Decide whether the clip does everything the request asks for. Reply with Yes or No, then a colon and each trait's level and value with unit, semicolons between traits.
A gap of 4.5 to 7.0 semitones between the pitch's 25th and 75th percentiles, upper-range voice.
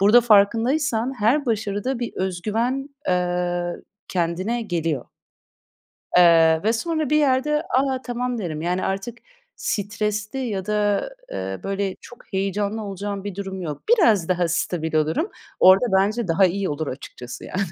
Yes: average, 5.1 semitones; high, 200 Hz